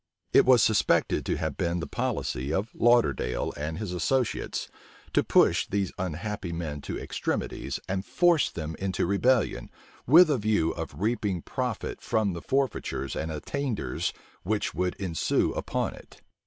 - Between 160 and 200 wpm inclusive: No, average, 150 wpm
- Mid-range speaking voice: No, very low, 95 Hz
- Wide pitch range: Yes, wide, 6.4 semitones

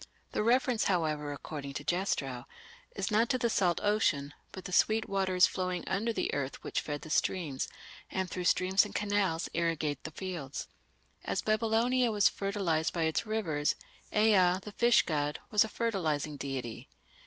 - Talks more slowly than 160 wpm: No, average, 165 wpm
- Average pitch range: No, wide, 5.7 semitones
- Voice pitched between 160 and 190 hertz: Yes, medium, 185 Hz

